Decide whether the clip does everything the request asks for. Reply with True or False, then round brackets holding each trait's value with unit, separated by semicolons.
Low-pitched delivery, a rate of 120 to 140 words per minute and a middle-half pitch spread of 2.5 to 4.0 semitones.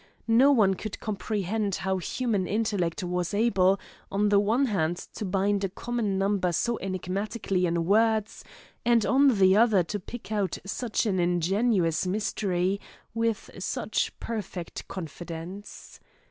False (200 Hz; 135 wpm; 3.2 semitones)